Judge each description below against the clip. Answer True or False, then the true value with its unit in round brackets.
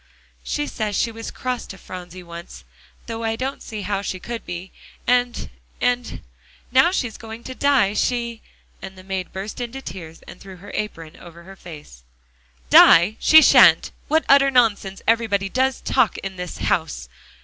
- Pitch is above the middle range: True (210 Hz)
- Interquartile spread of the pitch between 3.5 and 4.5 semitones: False (5.0 semitones)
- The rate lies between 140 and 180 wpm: True (170 wpm)